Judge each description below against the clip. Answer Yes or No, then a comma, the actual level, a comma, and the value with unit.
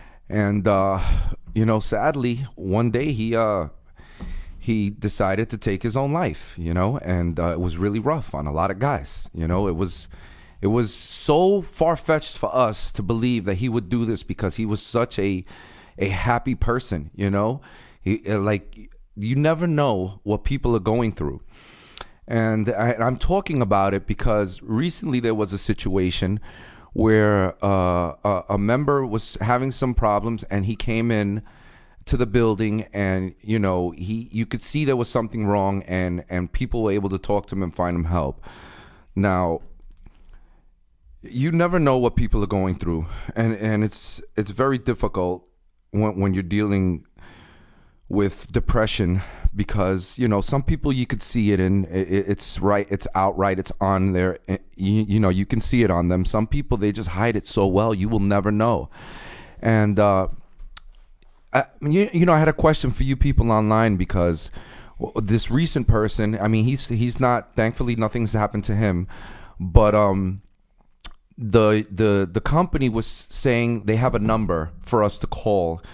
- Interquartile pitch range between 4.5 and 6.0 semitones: No, average, 3.8 semitones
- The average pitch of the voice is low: Yes, low, 105 Hz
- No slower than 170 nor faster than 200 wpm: Yes, average, 175 wpm